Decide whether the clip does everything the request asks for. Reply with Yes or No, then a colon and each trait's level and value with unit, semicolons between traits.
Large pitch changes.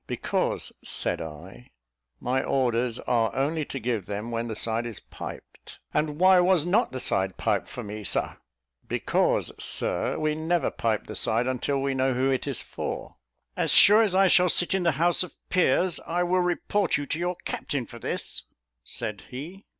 Yes: wide, 7.0 semitones